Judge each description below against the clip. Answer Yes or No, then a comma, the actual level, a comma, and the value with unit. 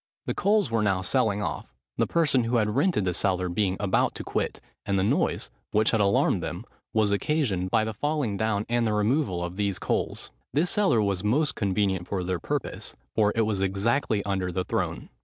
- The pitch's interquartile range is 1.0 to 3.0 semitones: No, average, 3.5 semitones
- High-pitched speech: No, low, 105 Hz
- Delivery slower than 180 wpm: No, average, 200 wpm